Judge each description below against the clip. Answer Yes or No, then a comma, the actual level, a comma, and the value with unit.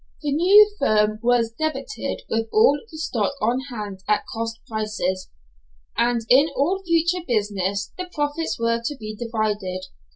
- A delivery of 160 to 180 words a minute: No, average, 150 wpm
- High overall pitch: Yes, high, 230 Hz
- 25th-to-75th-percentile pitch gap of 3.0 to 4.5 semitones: No, wide, 5.6 semitones